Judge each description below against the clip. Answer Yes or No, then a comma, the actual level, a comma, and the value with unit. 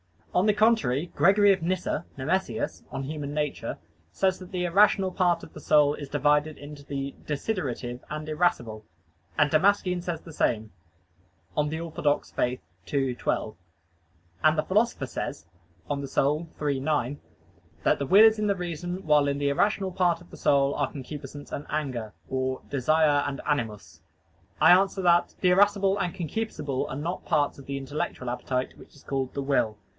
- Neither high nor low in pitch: Yes, medium, 150 Hz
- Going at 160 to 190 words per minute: Yes, average, 170 wpm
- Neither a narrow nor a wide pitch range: Yes, average, 4.7 semitones